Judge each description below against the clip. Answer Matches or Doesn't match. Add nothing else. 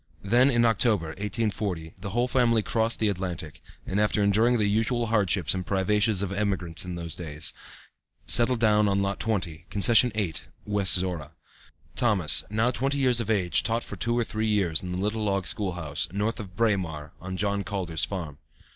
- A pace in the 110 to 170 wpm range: Doesn't match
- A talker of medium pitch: Doesn't match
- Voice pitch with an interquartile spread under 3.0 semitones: Doesn't match